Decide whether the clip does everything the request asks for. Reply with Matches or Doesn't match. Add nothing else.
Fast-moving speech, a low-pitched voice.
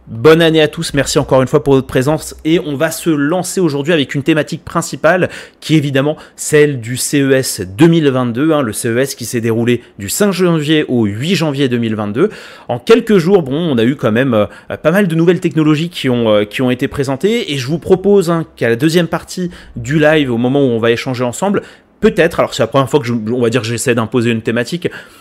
Doesn't match